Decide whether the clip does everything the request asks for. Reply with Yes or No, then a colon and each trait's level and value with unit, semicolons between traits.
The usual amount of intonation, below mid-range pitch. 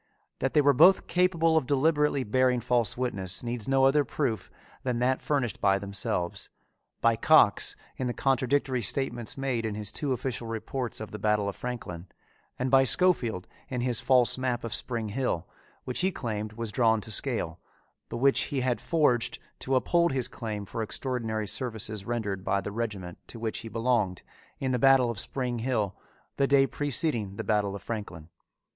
Yes: average, 3.8 semitones; low, 120 Hz